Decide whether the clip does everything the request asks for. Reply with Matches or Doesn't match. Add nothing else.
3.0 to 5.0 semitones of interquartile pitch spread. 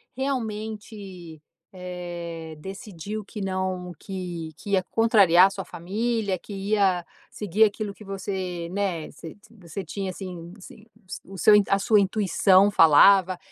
Doesn't match